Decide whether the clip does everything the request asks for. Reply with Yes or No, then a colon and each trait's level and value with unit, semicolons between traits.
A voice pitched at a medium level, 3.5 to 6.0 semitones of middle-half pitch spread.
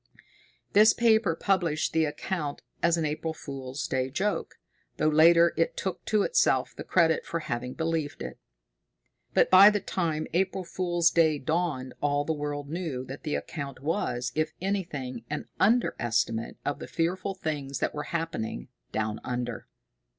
Yes: medium, 160 Hz; average, 4.1 semitones